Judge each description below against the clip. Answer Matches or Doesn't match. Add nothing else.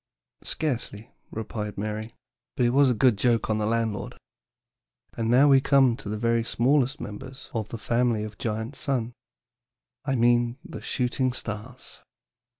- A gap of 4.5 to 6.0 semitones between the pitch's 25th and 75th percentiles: Doesn't match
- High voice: Doesn't match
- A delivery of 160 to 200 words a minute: Doesn't match